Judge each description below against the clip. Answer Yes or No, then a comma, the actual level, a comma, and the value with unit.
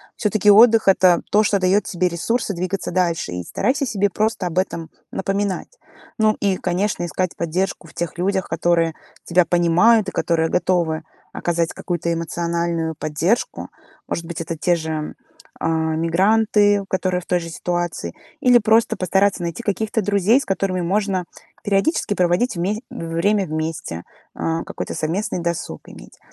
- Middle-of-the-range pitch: Yes, medium, 180 Hz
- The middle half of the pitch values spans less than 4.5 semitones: Yes, average, 3.4 semitones